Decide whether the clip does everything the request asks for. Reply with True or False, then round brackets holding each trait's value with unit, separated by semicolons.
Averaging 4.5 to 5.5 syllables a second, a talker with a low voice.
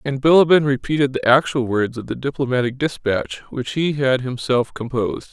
True (5.2 syllables/s; 130 Hz)